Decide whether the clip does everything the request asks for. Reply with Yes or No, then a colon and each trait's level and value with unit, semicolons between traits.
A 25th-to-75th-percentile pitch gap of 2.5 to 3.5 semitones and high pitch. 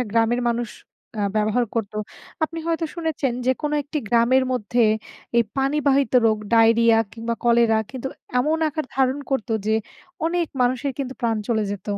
Yes: average, 3.2 semitones; high, 245 Hz